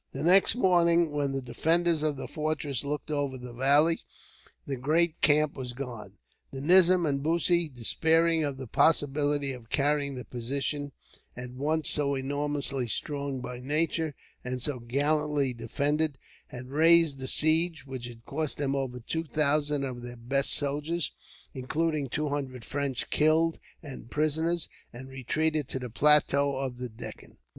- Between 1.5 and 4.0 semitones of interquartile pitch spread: Yes, average, 2.9 semitones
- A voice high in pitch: No, medium, 145 Hz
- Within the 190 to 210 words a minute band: No, average, 155 wpm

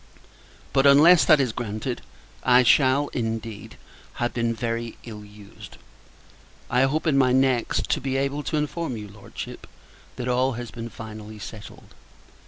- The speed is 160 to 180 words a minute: No, average, 150 wpm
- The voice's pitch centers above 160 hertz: No, low, 125 Hz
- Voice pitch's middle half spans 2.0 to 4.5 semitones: Yes, average, 3.3 semitones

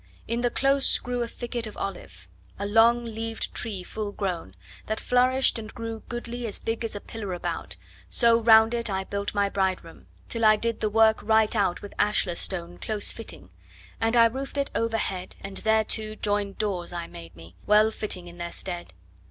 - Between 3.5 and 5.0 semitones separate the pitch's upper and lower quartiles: No, average, 2.8 semitones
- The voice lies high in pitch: Yes, high, 220 Hz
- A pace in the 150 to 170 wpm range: No, average, 195 wpm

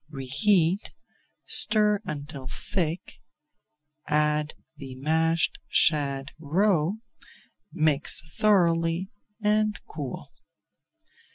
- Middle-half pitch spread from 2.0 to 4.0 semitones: No, average, 4.5 semitones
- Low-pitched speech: No, medium, 160 Hz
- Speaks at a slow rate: Yes, slow, 70 wpm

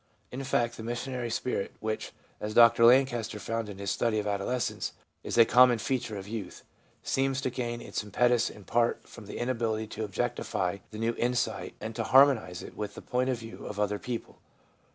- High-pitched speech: No, low, 115 Hz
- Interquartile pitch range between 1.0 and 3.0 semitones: Yes, narrow, 2.5 semitones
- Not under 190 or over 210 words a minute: Yes, average, 195 wpm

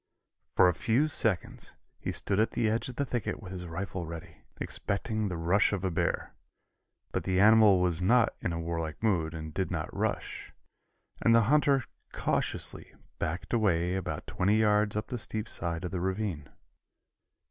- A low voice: Yes, very low, 95 Hz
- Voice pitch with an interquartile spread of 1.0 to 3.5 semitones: No, average, 4.2 semitones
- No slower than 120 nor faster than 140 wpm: No, average, 175 wpm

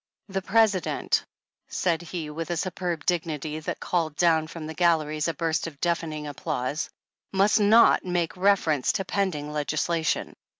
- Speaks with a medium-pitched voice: Yes, medium, 165 Hz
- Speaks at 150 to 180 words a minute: Yes, average, 155 wpm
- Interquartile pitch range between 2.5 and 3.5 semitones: Yes, average, 2.8 semitones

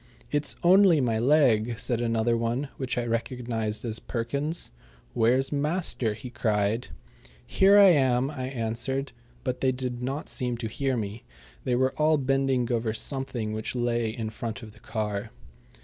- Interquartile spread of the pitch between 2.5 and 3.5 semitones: Yes, average, 3.0 semitones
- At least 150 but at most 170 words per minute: Yes, average, 160 wpm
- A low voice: Yes, low, 125 Hz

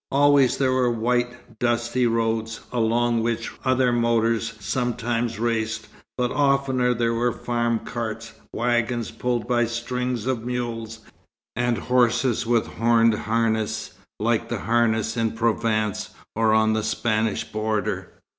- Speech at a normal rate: No, slow, 125 wpm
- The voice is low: Yes, low, 115 Hz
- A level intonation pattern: Yes, narrow, 1.5 semitones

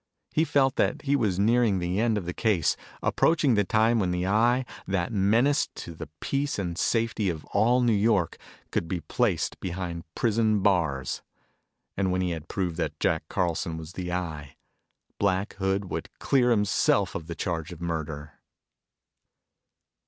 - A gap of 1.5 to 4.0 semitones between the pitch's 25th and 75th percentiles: No, average, 4.9 semitones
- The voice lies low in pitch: Yes, very low, 95 Hz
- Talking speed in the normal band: Yes, average, 165 wpm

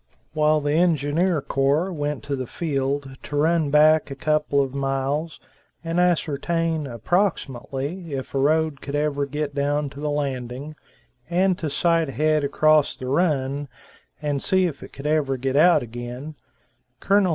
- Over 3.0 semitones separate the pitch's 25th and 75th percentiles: No, narrow, 2.5 semitones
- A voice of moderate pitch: Yes, medium, 145 Hz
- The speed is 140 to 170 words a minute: Yes, average, 155 wpm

